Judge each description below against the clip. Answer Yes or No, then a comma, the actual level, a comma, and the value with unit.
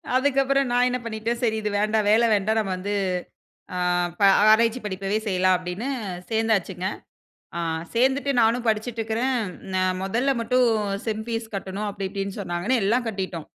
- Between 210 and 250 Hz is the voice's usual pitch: Yes, high, 220 Hz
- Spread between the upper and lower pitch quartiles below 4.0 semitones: Yes, average, 3.6 semitones